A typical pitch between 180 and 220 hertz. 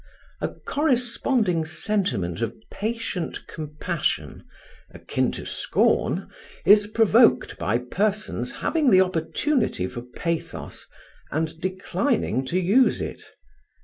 Yes: medium, 185 Hz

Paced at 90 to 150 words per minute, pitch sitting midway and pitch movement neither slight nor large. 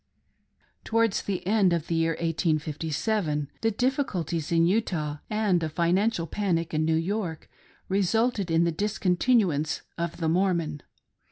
Yes: average, 140 wpm; medium, 170 Hz; average, 4.2 semitones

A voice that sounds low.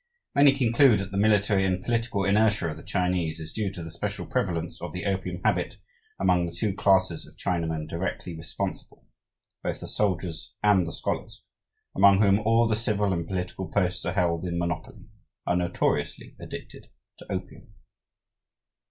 Yes: very low, 95 Hz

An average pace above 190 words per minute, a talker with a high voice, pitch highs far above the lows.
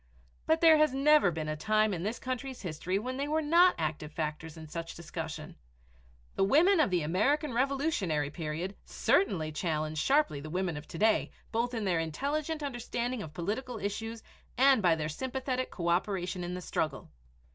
No: average, 175 wpm; high, 200 Hz; wide, 8.6 semitones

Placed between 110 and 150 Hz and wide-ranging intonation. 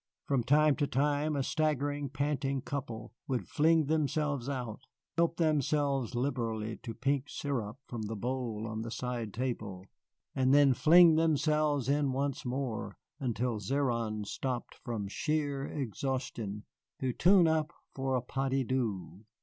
No: low, 135 Hz; average, 3.8 semitones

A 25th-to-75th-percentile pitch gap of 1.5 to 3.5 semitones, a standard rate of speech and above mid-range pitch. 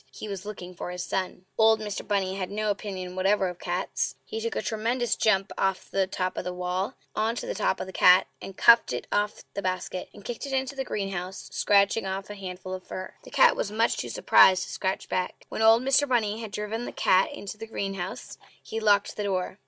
No: average, 2.8 semitones; fast, 230 wpm; high, 200 Hz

